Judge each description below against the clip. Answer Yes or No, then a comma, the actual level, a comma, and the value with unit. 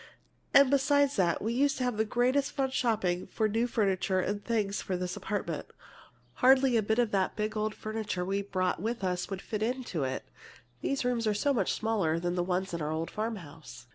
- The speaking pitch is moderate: No, high, 215 Hz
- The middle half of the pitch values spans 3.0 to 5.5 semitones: Yes, average, 4.8 semitones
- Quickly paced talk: Yes, fast, 210 wpm